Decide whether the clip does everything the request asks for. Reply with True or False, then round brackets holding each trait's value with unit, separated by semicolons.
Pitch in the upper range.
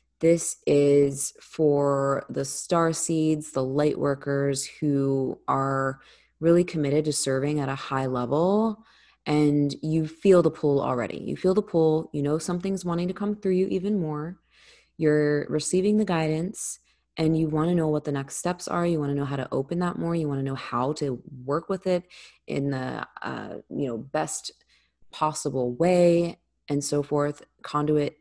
False (150 Hz)